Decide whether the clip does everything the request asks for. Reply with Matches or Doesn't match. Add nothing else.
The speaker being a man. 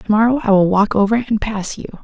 Doesn't match